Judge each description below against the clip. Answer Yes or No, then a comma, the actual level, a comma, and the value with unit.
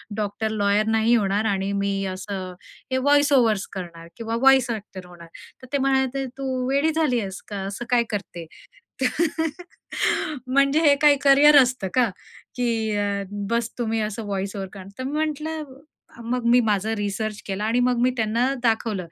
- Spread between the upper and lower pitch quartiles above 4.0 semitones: Yes, average, 4.7 semitones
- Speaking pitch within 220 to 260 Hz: Yes, high, 225 Hz